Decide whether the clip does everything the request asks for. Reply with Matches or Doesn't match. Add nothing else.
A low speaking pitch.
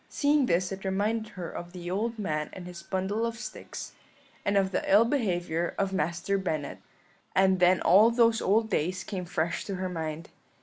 Doesn't match